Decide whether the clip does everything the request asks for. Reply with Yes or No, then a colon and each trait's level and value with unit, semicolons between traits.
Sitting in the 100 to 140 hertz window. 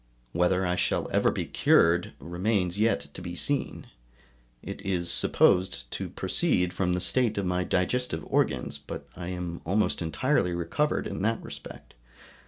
No: very low, 90 Hz